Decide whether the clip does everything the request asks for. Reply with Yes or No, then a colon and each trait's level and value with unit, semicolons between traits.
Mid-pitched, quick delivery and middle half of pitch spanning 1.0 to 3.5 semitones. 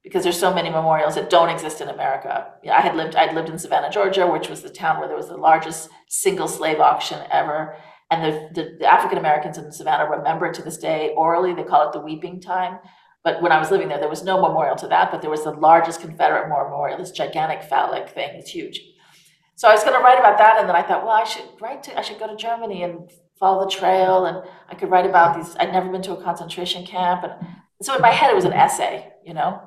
Yes: medium, 175 Hz; fast, 255 wpm; average, 3.0 semitones